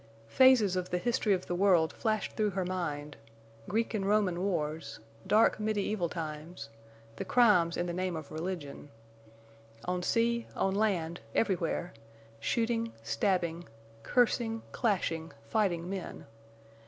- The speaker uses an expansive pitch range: No, average, 4.7 semitones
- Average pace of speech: No, slow, 120 wpm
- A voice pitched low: No, medium, 180 Hz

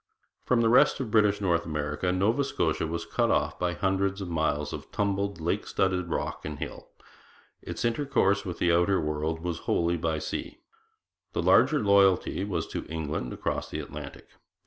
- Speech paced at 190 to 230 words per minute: No, average, 170 wpm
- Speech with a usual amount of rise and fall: Yes, average, 3.8 semitones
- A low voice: Yes, very low, 90 Hz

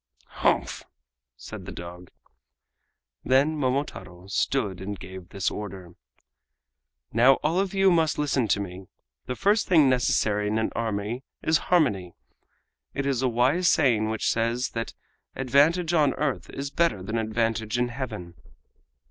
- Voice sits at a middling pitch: No, low, 120 Hz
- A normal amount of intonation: No, wide, 5.7 semitones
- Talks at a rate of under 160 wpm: Yes, average, 140 wpm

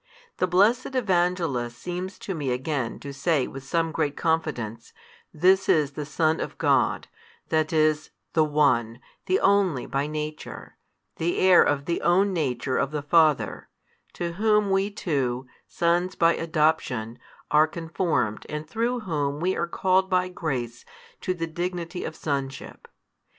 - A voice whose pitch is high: No, medium, 160 Hz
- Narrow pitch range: No, average, 4.4 semitones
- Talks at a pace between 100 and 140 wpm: No, average, 150 wpm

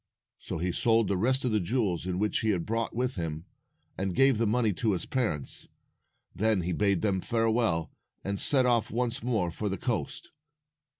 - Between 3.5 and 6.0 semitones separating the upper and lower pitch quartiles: Yes, average, 4.4 semitones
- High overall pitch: No, low, 105 Hz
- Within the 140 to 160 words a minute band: No, average, 185 wpm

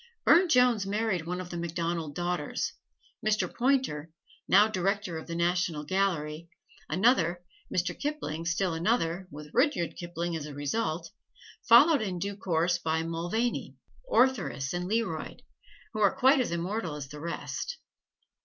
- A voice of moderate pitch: Yes, medium, 175 Hz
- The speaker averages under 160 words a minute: Yes, average, 145 wpm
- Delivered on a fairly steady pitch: No, average, 4.7 semitones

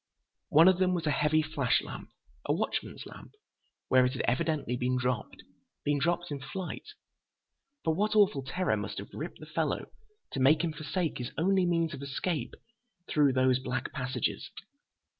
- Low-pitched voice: No, medium, 150 Hz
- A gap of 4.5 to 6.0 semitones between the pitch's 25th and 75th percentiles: Yes, average, 4.9 semitones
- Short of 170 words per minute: Yes, average, 160 wpm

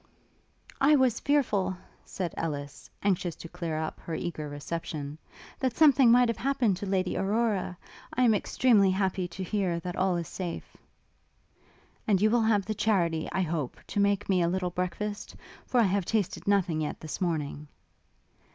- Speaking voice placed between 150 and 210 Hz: Yes, high, 190 Hz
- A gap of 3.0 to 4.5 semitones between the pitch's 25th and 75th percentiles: Yes, average, 4.2 semitones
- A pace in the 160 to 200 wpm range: Yes, average, 170 wpm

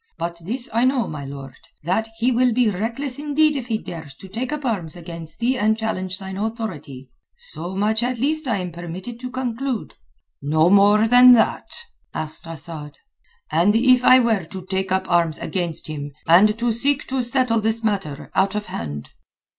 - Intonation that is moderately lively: No, wide, 6.2 semitones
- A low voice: No, high, 210 Hz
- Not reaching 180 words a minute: No, average, 185 wpm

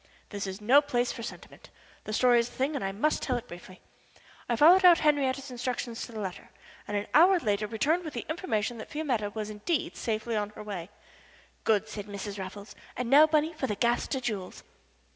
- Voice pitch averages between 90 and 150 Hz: No, high, 235 Hz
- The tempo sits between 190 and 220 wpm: Yes, fast, 205 wpm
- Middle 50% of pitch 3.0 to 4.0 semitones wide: No, wide, 5.5 semitones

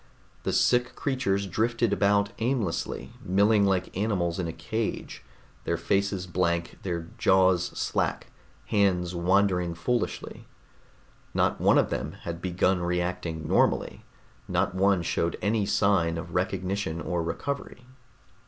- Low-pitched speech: Yes, very low, 95 Hz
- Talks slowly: Yes, slow, 125 wpm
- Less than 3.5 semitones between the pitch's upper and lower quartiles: Yes, average, 2.9 semitones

